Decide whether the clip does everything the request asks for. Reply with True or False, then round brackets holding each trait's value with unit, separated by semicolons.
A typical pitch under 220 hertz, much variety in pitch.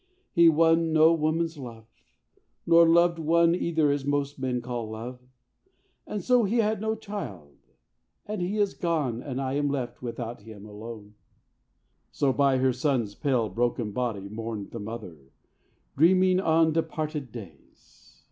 True (140 Hz; 6.2 semitones)